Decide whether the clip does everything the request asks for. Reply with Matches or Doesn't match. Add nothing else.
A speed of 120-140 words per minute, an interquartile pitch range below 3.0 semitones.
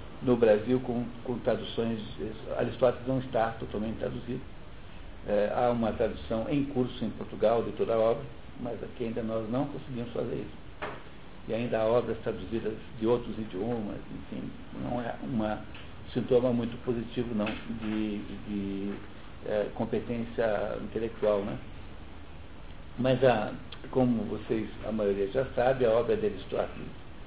Matches